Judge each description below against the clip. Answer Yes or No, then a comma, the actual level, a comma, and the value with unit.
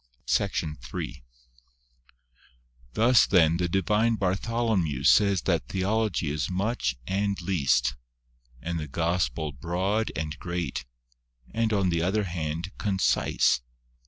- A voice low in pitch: Yes, very low, 90 Hz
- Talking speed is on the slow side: Yes, slow, 120 wpm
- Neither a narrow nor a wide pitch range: Yes, average, 4.5 semitones